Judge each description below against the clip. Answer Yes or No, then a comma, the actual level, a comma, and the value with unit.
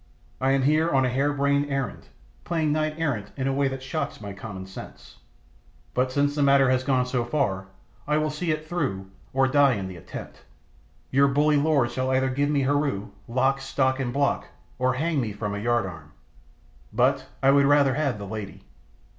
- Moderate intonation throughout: Yes, average, 3.2 semitones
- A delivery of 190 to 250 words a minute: Yes, average, 195 wpm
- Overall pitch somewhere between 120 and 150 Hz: Yes, low, 135 Hz